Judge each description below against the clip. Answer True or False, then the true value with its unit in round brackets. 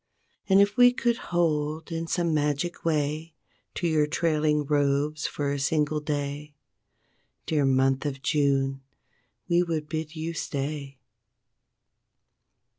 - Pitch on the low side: False (150 Hz)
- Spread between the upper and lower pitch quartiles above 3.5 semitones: False (2.4 semitones)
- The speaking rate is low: True (120 wpm)